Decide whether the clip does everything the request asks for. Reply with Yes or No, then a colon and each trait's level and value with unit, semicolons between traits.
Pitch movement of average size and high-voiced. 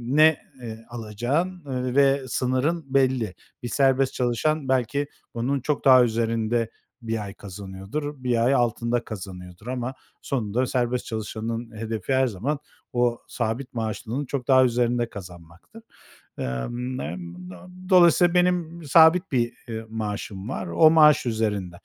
No: average, 3.7 semitones; low, 120 Hz